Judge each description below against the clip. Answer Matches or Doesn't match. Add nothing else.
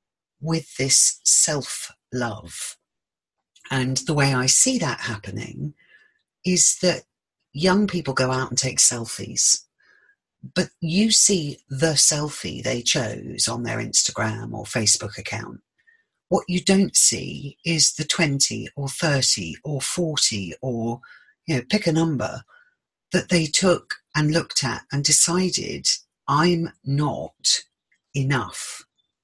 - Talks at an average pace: Doesn't match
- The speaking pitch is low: Doesn't match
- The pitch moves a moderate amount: Doesn't match